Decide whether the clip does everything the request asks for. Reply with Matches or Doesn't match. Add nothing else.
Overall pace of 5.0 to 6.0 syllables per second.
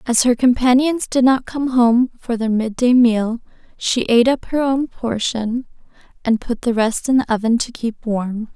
Doesn't match